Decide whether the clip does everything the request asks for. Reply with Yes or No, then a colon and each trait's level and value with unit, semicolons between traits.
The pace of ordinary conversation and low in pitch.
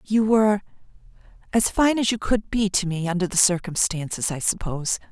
No: average, 165 wpm; high, 195 Hz